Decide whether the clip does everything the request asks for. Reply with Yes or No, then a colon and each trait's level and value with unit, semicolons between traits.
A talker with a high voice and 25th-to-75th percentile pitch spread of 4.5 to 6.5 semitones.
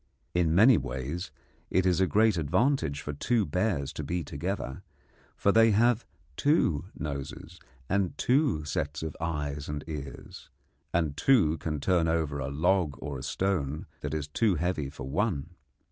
No: very low, 80 Hz; average, 5.1 semitones